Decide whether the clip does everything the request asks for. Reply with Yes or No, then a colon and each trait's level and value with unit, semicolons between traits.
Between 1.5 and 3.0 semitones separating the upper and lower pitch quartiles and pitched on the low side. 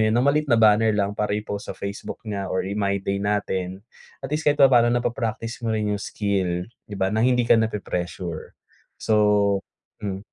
Yes: narrow, 2.4 semitones; low, 105 Hz